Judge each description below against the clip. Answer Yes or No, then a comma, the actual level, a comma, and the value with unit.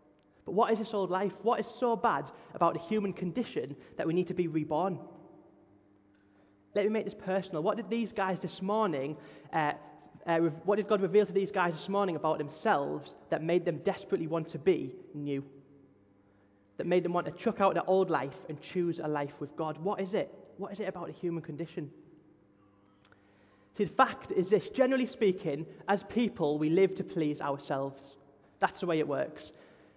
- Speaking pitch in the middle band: Yes, medium, 175 Hz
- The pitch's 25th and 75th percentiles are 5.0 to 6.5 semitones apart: Yes, wide, 5.5 semitones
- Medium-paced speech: Yes, average, 195 wpm